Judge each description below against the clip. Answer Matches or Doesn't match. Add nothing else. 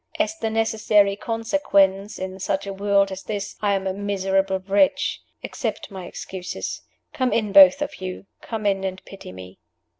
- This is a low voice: Doesn't match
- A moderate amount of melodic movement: Doesn't match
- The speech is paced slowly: Doesn't match